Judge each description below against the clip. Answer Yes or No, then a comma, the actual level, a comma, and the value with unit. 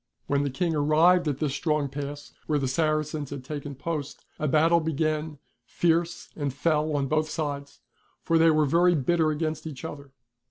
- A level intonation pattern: Yes, narrow, 2.1 semitones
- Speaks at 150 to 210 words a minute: Yes, average, 175 wpm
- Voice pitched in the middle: Yes, medium, 155 Hz